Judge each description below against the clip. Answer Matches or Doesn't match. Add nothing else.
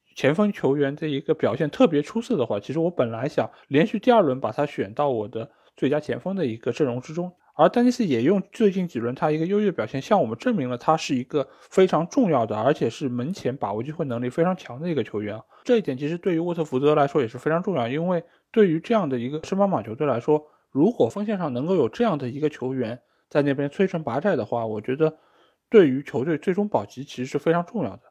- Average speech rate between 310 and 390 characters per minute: Matches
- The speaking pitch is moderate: Matches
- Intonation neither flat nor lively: Doesn't match